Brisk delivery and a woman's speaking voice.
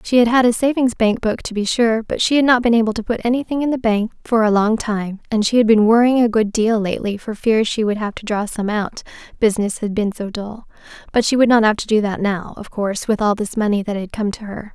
Yes: fast, 275 wpm; female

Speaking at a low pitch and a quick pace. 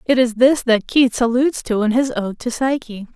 No: high, 245 Hz; fast, 230 wpm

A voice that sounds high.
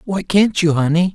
No: medium, 175 Hz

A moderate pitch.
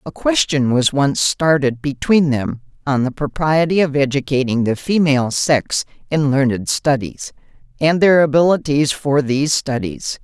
Yes: medium, 145 Hz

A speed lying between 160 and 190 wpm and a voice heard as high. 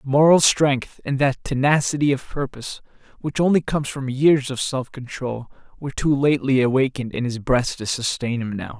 No: average, 175 wpm; low, 135 Hz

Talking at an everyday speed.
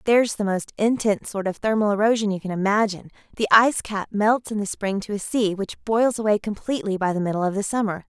No: fast, 220 wpm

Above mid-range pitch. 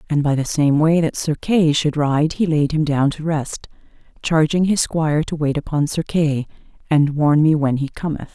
No: medium, 150 Hz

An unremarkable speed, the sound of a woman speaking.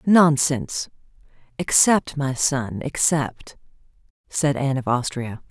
No: slow, 100 wpm; female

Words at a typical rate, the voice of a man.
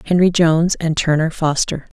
No: average, 150 wpm; female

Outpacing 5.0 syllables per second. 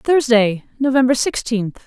No: 4.1 syllables/s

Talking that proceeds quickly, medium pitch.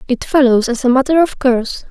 No: fast, 220 wpm; very high, 255 Hz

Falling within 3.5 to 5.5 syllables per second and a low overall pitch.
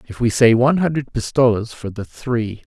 Yes: 5.2 syllables/s; low, 120 Hz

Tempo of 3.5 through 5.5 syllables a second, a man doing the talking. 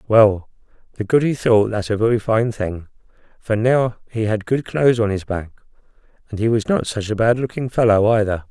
Yes: 5.3 syllables/s; male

